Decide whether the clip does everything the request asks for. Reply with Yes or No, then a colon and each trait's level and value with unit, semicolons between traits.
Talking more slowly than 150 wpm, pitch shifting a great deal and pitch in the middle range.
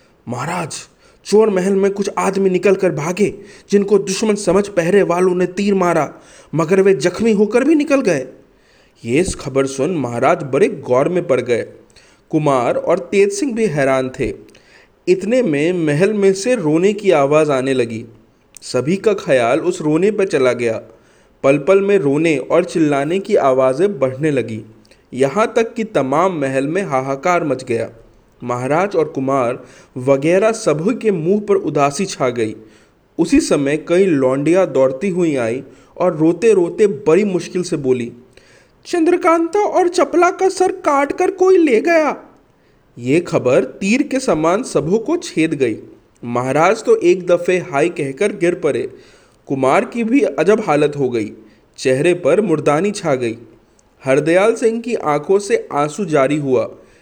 No: average, 160 wpm; wide, 7.6 semitones; medium, 180 Hz